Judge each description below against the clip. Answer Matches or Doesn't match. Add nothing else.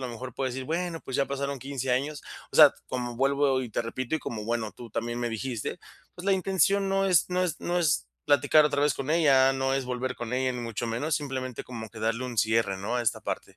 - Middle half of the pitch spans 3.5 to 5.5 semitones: Matches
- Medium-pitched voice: Doesn't match